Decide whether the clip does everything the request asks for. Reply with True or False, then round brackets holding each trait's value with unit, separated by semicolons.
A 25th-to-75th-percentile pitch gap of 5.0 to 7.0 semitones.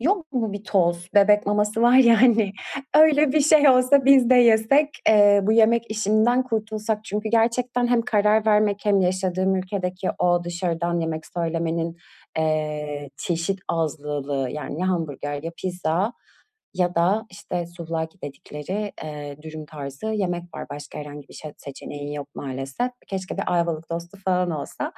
True (5.3 semitones)